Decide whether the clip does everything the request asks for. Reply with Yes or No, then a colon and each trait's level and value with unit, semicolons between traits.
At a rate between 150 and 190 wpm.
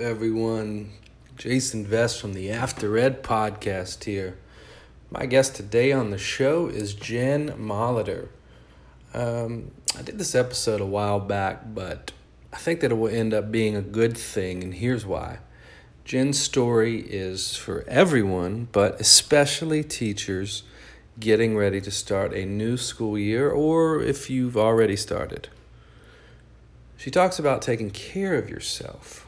No: average, 140 wpm